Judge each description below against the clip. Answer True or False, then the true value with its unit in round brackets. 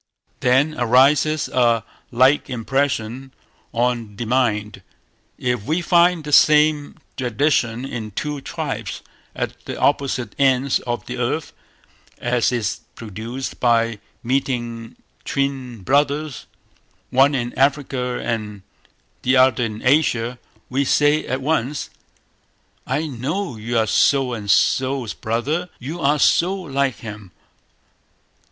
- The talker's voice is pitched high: False (130 Hz)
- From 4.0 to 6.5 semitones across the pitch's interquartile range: False (3.4 semitones)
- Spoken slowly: True (120 wpm)